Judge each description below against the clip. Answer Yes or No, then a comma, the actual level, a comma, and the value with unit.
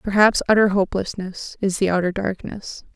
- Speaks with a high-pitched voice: Yes, high, 195 Hz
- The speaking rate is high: No, average, 140 wpm